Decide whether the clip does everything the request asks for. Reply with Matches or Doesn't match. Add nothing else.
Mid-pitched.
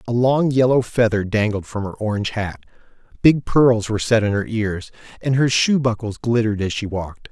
Doesn't match